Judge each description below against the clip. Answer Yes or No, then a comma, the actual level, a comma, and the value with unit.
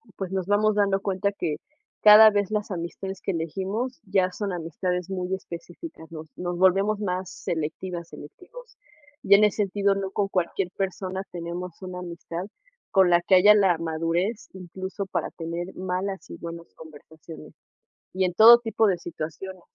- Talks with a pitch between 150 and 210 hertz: Yes, medium, 185 Hz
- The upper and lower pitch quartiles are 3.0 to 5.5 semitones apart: No, narrow, 2.6 semitones